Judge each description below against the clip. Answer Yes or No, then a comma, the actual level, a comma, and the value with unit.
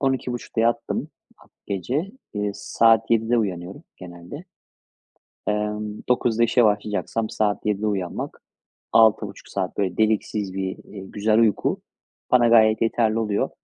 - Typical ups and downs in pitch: No, narrow, 2.2 semitones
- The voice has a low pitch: Yes, low, 110 Hz